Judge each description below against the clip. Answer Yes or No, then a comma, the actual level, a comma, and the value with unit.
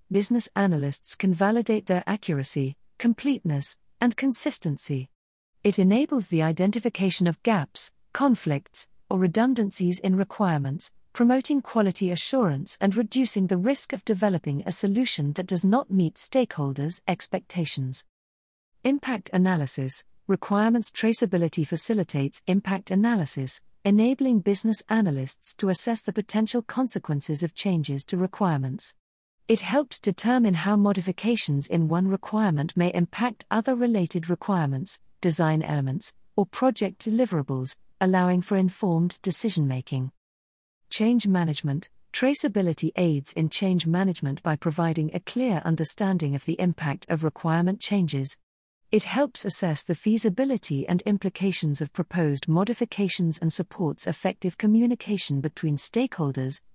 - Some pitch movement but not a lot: No, wide, 5.7 semitones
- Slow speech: Yes, slow, 120 wpm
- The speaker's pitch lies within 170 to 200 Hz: Yes, medium, 185 Hz